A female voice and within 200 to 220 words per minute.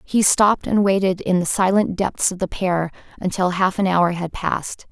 Yes: female; fast, 205 wpm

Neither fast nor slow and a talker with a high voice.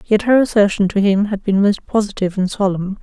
No: fast, 220 wpm; high, 205 Hz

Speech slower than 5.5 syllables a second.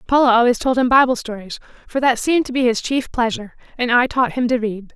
No: 6.2 syllables/s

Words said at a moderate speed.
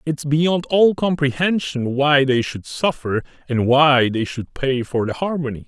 Yes: average, 170 wpm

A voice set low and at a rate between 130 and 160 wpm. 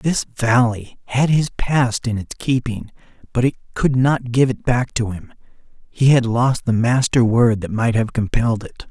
No: low, 120 Hz; average, 190 wpm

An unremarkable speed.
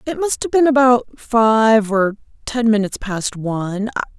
Yes: average, 160 wpm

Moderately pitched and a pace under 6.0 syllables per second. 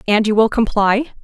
No: high, 220 Hz; 5.3 syllables/s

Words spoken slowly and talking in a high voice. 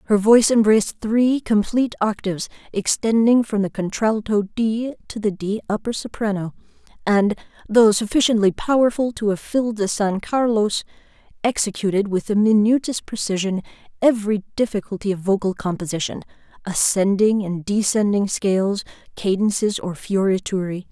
Yes: slow, 125 wpm; high, 210 Hz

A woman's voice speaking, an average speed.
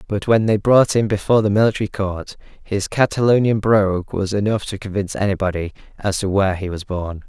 No: male; average, 190 wpm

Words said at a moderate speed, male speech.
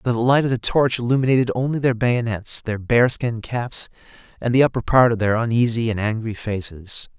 Yes: average, 190 wpm; male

